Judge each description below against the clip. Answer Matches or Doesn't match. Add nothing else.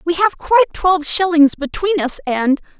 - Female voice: Matches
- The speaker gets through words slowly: Doesn't match